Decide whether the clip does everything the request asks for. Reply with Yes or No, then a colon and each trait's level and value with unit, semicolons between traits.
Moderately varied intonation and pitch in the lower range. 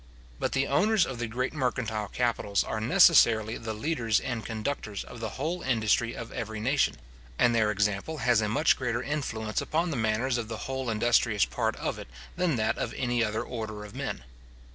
Yes: average, 3.4 semitones; low, 115 Hz